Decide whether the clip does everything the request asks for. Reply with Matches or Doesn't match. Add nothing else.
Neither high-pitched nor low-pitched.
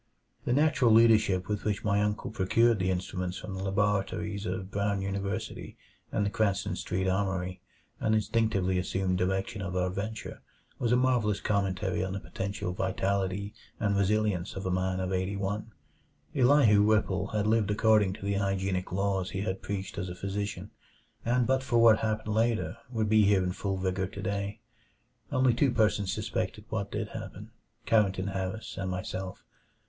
Doesn't match